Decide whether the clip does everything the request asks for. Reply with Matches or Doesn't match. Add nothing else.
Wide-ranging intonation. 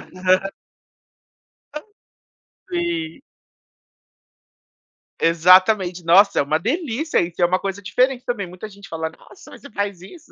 Matches